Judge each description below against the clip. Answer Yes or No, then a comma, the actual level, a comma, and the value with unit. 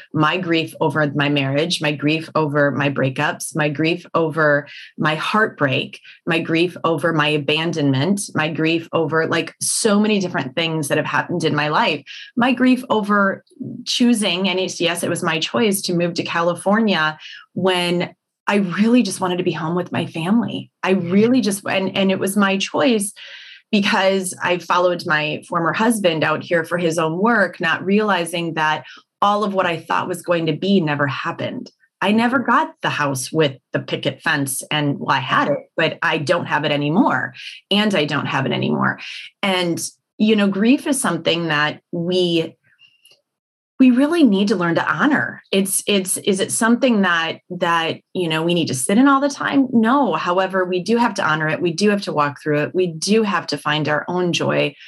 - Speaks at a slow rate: No, average, 195 wpm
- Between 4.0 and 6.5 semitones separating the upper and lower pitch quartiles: Yes, average, 4.4 semitones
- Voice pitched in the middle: Yes, medium, 175 Hz